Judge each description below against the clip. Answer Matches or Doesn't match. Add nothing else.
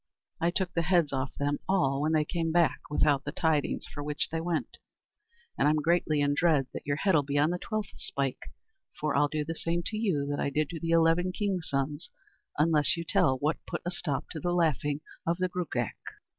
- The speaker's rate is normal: Doesn't match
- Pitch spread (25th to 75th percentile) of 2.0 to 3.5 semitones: Matches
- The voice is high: Doesn't match